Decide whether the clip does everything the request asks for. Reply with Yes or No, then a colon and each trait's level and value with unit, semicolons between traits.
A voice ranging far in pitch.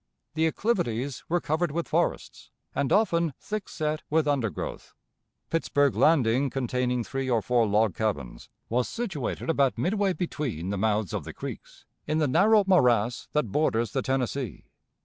Yes: wide, 5.7 semitones